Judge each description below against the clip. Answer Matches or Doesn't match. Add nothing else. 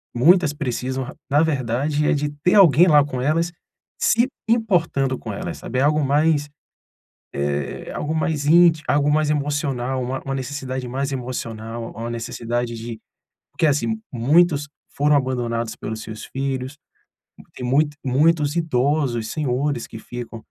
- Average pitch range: Matches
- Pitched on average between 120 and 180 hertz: Matches